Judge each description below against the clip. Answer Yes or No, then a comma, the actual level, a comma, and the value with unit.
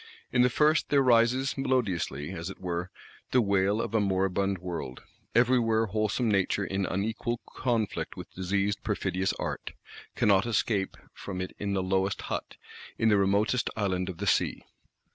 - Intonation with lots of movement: No, average, 3.7 semitones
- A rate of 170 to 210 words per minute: No, average, 160 wpm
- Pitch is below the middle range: Yes, low, 100 Hz